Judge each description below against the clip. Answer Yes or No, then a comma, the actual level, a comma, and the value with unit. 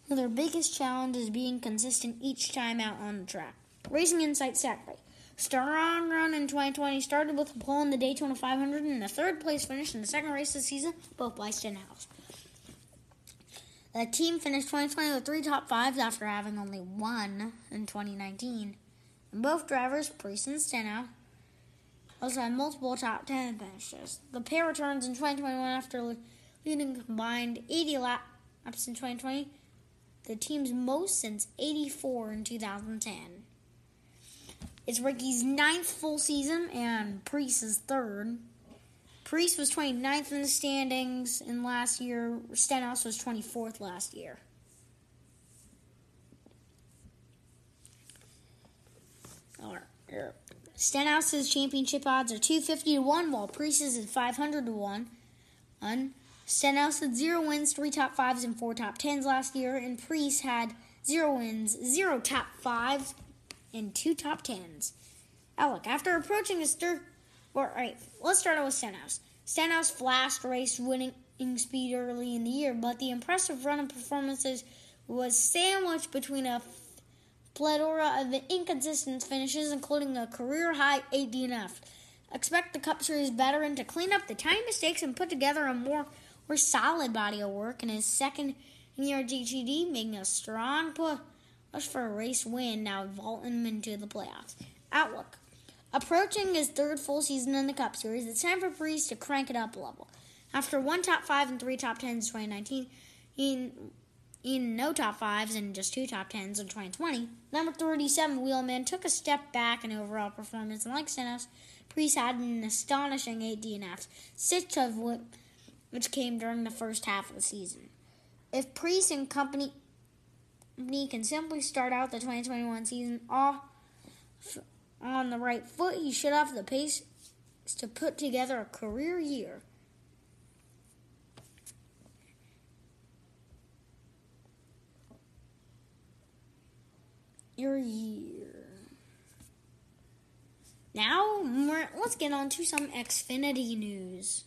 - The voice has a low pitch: No, very high, 265 Hz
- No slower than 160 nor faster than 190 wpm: No, average, 145 wpm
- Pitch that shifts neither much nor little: Yes, average, 3.9 semitones